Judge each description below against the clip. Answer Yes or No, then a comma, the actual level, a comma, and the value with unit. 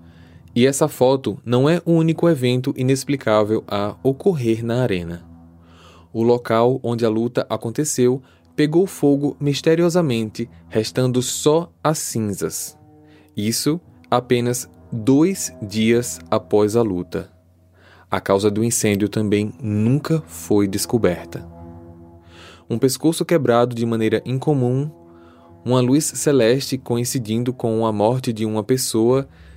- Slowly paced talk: Yes, slow, 115 wpm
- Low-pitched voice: Yes, low, 115 Hz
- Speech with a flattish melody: No, average, 4.9 semitones